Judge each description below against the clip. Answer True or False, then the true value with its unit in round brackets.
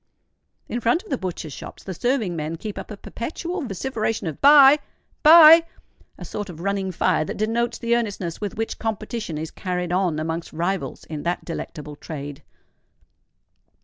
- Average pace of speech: True (160 wpm)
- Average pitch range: False (6.1 semitones)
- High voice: True (200 Hz)